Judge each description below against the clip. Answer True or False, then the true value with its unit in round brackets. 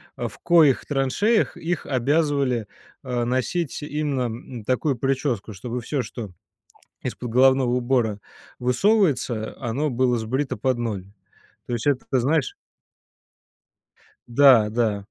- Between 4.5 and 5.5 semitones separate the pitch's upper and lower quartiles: False (3.3 semitones)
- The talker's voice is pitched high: False (125 Hz)